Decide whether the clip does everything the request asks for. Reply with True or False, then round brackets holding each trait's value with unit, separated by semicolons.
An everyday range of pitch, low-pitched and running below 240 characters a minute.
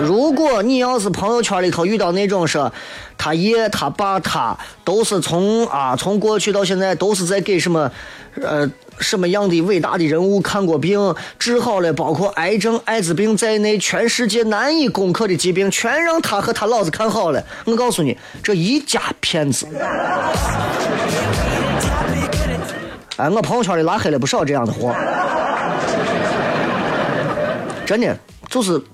False (4.1 semitones; 200 Hz; 230 characters per minute)